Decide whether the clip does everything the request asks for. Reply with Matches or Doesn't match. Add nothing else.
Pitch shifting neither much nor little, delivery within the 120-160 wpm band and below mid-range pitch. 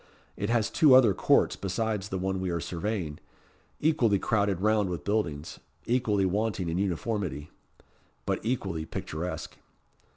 Matches